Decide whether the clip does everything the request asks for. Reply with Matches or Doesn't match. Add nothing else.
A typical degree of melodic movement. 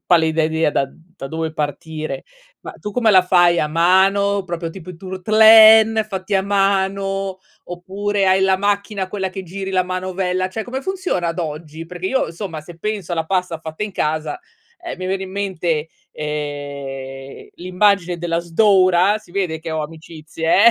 Matches